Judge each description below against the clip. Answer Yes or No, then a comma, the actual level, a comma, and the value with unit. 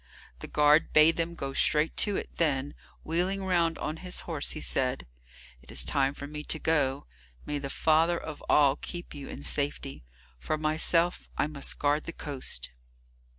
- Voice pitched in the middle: Yes, medium, 150 Hz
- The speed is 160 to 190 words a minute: Yes, average, 175 wpm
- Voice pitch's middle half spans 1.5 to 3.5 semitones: Yes, average, 2.7 semitones